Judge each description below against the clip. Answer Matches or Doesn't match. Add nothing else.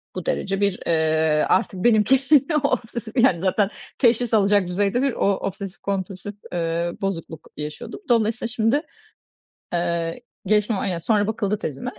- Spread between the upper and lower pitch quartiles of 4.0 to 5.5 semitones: Matches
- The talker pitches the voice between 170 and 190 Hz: Doesn't match